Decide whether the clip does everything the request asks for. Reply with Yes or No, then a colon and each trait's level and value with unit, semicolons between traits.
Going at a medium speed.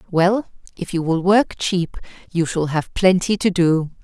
Yes: average, 180 wpm